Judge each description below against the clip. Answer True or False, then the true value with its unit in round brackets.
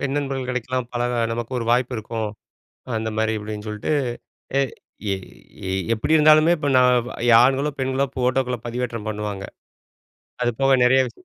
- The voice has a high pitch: False (125 Hz)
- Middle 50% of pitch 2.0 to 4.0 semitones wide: True (3.0 semitones)